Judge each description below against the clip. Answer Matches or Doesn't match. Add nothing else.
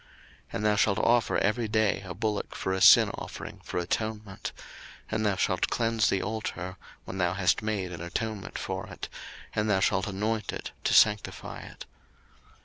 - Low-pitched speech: Matches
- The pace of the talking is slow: Doesn't match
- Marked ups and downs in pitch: Doesn't match